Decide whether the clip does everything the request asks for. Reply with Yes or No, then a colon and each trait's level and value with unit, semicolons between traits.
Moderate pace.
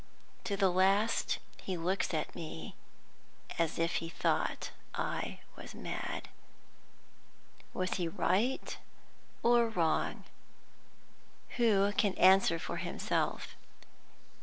No: slow, 100 wpm